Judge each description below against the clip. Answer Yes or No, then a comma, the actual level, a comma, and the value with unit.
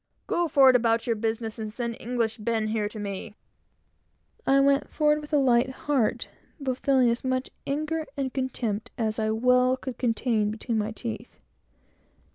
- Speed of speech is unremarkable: Yes, average, 170 wpm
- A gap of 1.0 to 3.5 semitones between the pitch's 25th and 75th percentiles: Yes, average, 3.0 semitones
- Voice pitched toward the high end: Yes, high, 240 Hz